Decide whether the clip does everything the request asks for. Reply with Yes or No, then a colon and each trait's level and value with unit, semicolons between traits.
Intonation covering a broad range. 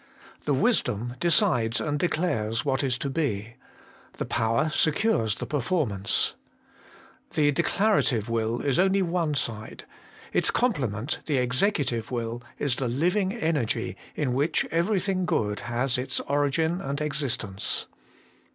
Yes: wide, 6.1 semitones